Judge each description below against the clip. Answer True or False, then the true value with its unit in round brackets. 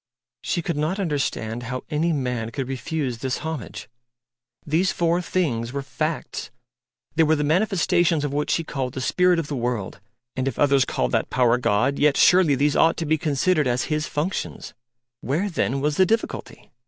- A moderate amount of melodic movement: True (4.2 semitones)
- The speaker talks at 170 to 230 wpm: True (180 wpm)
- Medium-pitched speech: True (150 Hz)